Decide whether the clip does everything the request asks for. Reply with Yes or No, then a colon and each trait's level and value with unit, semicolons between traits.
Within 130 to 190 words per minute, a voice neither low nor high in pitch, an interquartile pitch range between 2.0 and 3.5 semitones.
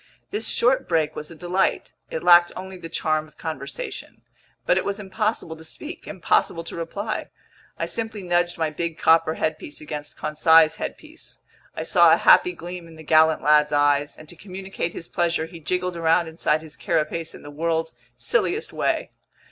Yes: average, 180 wpm; medium, 165 Hz; average, 2.8 semitones